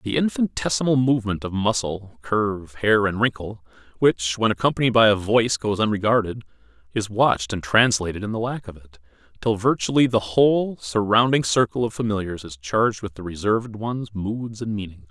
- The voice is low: Yes, low, 110 Hz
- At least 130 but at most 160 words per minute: No, average, 170 wpm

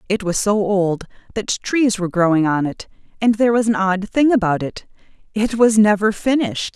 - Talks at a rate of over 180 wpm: Yes, average, 195 wpm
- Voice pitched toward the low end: No, high, 205 Hz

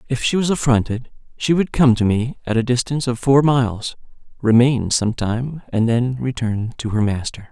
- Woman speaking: No, male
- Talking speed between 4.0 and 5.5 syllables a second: Yes, 5.0 syllables/s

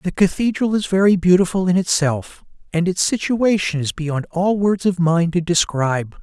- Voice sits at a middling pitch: Yes, medium, 180 Hz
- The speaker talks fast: No, average, 175 wpm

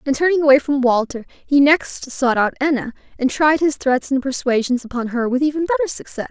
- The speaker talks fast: Yes, fast, 210 wpm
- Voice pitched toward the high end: Yes, very high, 270 Hz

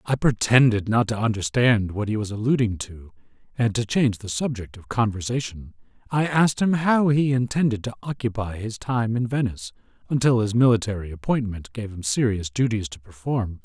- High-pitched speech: No, low, 115 Hz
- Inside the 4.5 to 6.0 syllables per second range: Yes, 5.4 syllables/s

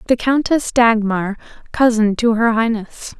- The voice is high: Yes, high, 230 Hz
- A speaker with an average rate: No, slow, 130 wpm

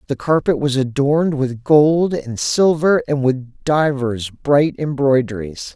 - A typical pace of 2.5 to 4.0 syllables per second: Yes, 3.8 syllables/s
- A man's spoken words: Yes, male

